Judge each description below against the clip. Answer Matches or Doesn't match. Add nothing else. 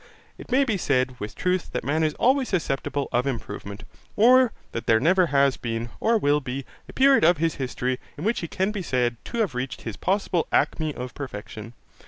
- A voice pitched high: Doesn't match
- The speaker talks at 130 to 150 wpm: Doesn't match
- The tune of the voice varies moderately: Doesn't match